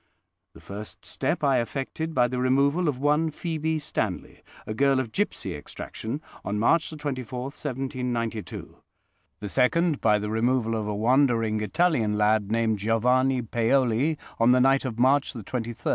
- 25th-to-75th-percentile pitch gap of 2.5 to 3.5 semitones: No, average, 4.1 semitones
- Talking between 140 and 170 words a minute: Yes, average, 155 wpm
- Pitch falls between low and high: No, low, 125 Hz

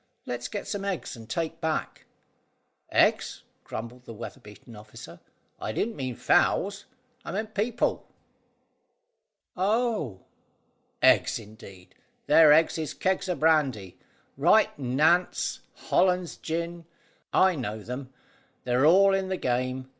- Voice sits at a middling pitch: Yes, medium, 155 Hz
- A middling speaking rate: No, slow, 125 wpm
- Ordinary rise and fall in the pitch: No, wide, 7.4 semitones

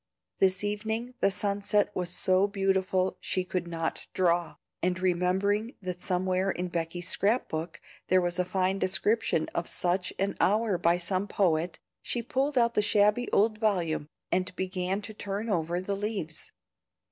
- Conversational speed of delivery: Yes, average, 160 wpm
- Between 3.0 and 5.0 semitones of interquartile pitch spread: No, narrow, 2.4 semitones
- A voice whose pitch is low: No, medium, 185 Hz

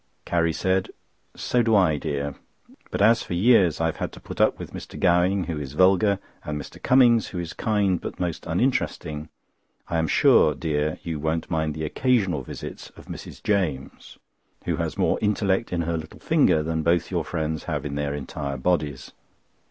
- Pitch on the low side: Yes, very low, 85 Hz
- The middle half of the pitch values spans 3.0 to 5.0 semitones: Yes, average, 3.8 semitones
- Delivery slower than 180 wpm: No, average, 185 wpm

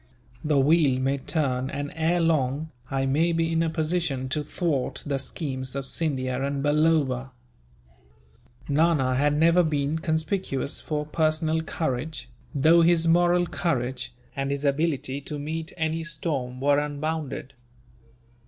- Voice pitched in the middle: Yes, medium, 150 Hz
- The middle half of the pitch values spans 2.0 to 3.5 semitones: Yes, average, 3.0 semitones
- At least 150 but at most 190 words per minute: No, slow, 135 wpm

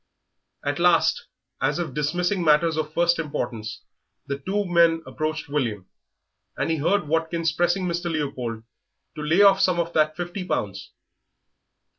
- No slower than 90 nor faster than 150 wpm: Yes, average, 145 wpm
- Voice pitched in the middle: Yes, medium, 160 Hz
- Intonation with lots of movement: No, average, 3.0 semitones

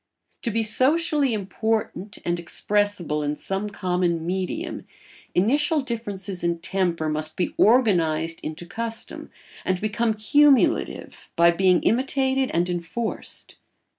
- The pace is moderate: No, slow, 115 wpm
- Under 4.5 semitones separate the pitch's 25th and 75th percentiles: No, average, 5.1 semitones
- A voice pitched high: Yes, high, 195 Hz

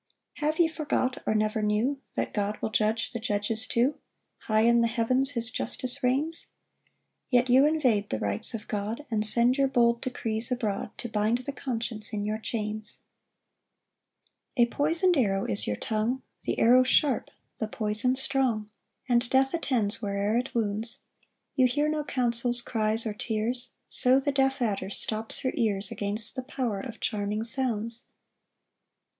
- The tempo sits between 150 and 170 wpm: Yes, average, 165 wpm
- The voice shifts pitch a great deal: No, average, 3.3 semitones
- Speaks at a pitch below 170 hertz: No, high, 235 Hz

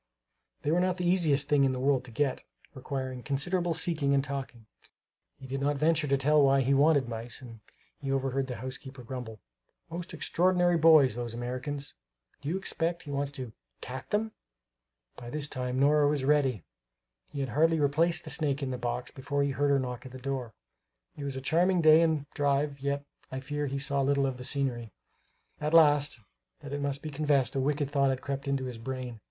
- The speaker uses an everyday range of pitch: No, narrow, 2.3 semitones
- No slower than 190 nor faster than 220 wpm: Yes, average, 200 wpm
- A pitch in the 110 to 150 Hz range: Yes, medium, 140 Hz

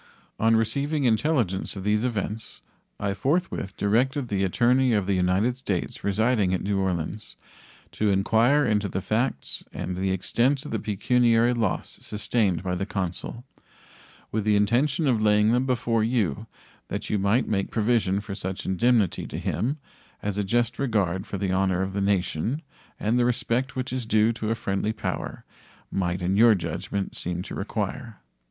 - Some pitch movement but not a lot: Yes, average, 3.7 semitones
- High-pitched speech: No, low, 105 Hz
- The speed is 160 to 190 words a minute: Yes, average, 170 wpm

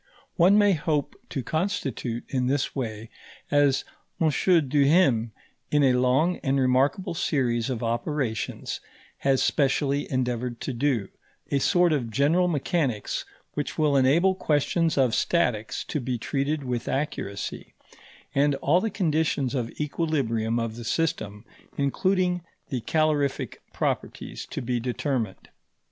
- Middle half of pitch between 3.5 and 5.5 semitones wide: Yes, average, 4.1 semitones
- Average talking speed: No, slow, 130 wpm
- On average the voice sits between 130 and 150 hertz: Yes, medium, 140 Hz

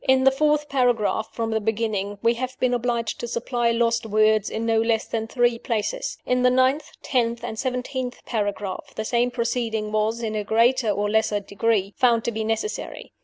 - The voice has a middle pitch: No, high, 230 Hz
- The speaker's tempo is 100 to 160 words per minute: No, average, 190 wpm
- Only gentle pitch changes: Yes, narrow, 2.2 semitones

